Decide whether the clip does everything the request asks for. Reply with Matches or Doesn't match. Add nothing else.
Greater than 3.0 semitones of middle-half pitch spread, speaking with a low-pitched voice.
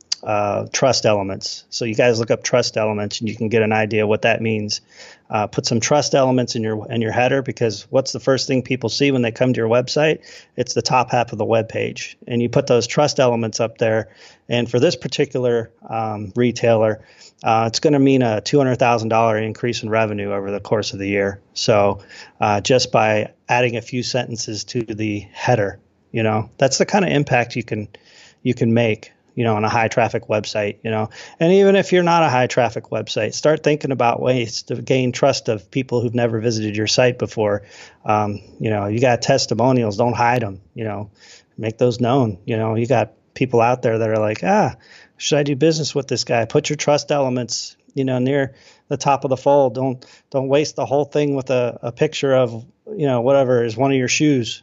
Matches